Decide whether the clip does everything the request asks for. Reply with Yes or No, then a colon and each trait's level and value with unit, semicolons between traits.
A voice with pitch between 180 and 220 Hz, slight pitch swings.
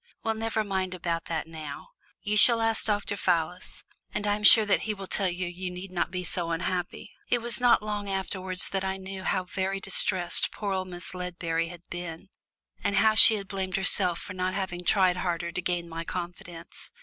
Yes: medium, 185 Hz; narrow, 2.3 semitones